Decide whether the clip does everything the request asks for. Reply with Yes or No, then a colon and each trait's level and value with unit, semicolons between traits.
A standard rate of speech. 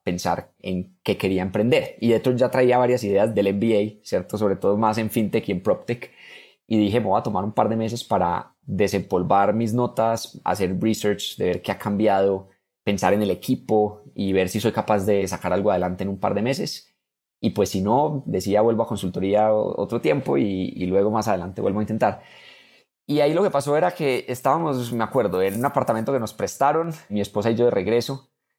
No: fast, 215 wpm